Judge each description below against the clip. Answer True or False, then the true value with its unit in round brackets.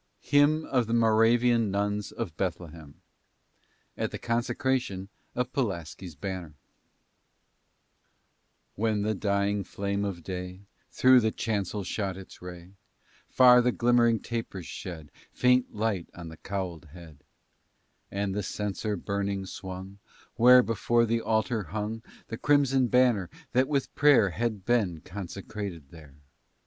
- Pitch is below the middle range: True (105 Hz)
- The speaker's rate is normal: False (125 wpm)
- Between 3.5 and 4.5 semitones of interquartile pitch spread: True (4.2 semitones)